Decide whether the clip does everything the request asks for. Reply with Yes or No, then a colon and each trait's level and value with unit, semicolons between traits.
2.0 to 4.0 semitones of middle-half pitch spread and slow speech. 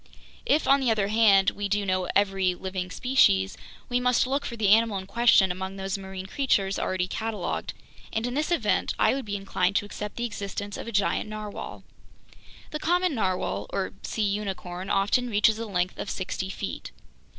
No: average, 3.3 semitones; average, 185 wpm